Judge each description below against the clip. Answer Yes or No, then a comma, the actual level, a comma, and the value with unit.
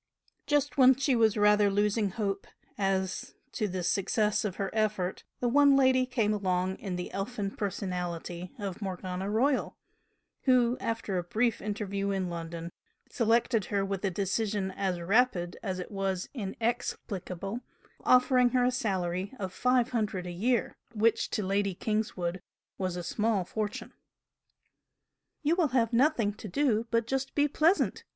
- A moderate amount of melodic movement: Yes, average, 4.1 semitones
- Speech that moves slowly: No, average, 150 wpm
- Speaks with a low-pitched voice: No, high, 205 Hz